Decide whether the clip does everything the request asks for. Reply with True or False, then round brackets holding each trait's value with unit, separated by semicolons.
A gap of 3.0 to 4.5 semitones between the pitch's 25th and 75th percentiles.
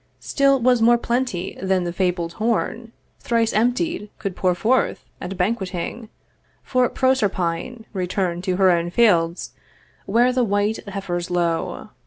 False (4.9 semitones)